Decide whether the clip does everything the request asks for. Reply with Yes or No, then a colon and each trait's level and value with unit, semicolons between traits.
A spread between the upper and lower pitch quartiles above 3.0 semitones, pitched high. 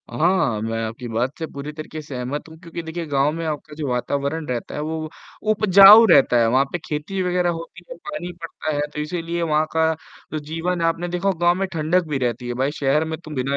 No: average, 3.6 semitones; medium, 155 Hz